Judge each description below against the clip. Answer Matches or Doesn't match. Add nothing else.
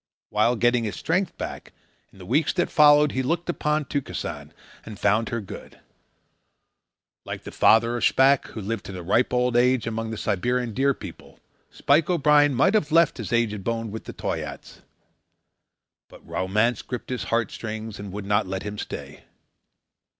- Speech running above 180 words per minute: Doesn't match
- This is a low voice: Matches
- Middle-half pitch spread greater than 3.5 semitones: Matches